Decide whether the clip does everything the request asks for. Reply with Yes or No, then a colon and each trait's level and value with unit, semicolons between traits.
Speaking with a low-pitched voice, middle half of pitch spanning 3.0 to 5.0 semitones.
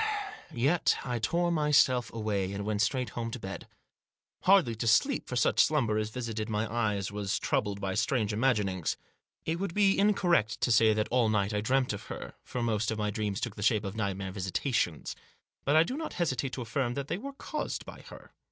Yes: low, 115 Hz; average, 4.6 semitones